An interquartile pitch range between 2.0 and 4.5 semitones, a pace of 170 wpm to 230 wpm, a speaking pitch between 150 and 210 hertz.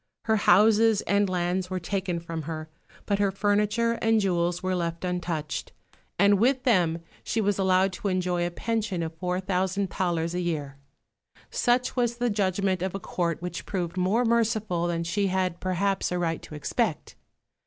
Yes: average, 2.9 semitones; average, 175 wpm; medium, 185 Hz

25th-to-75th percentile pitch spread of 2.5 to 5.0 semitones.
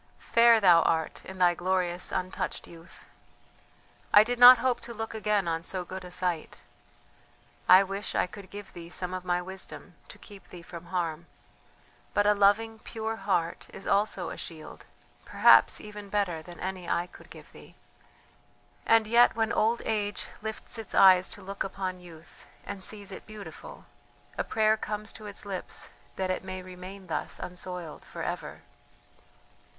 Yes: average, 2.9 semitones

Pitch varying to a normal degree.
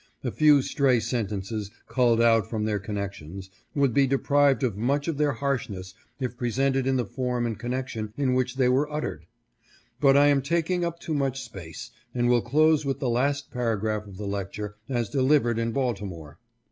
Yes: average, 4.5 semitones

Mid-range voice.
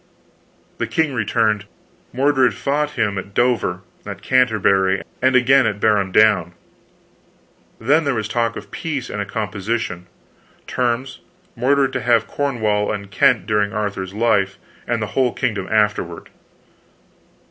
No: low, 110 Hz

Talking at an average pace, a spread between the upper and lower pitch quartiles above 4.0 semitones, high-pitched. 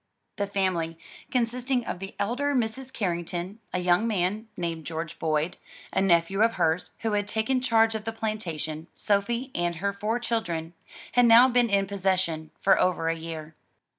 Yes: average, 165 wpm; average, 5.0 semitones; high, 200 Hz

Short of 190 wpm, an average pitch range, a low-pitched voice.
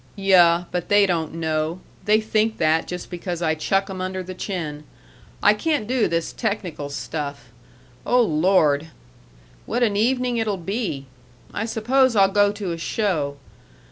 No: average, 155 wpm; average, 4.7 semitones; medium, 185 Hz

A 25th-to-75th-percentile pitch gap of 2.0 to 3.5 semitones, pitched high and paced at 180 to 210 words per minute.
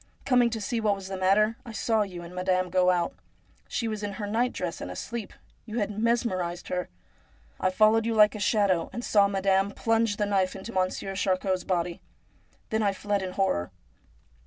Yes: average, 2.9 semitones; high, 200 Hz; average, 190 wpm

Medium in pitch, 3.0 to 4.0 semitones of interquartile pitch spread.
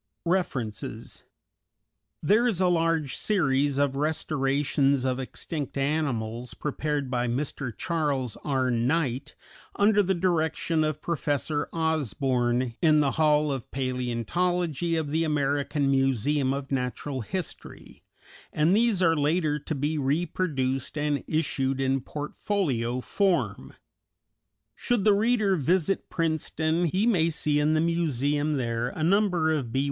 Yes: medium, 150 Hz; average, 3.7 semitones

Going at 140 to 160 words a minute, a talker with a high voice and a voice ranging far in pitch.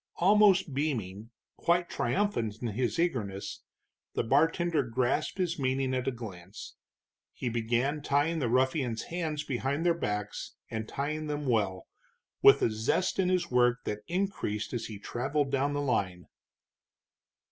No: average, 145 wpm; low, 130 Hz; wide, 5.7 semitones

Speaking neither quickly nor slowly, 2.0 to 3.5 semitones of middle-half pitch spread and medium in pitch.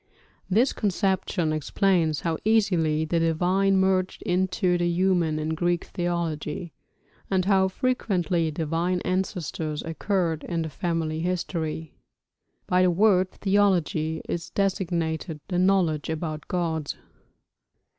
No: slow, 110 wpm; average, 2.9 semitones; medium, 175 Hz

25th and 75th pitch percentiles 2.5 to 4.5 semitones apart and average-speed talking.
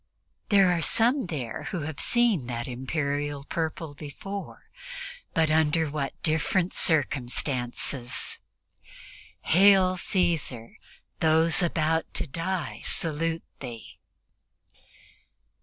No: average, 3.7 semitones; slow, 90 wpm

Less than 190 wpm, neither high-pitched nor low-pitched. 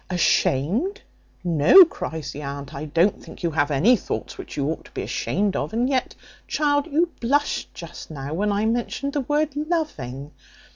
No: average, 180 wpm; high, 200 Hz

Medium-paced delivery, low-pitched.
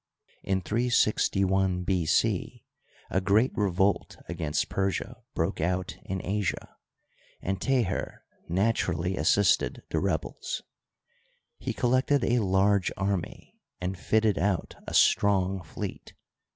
No: slow, 110 wpm; very low, 95 Hz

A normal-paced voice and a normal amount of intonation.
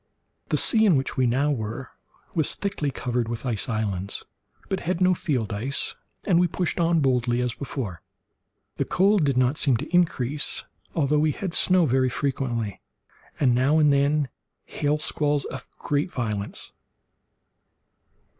Yes: average, 155 wpm; average, 4.3 semitones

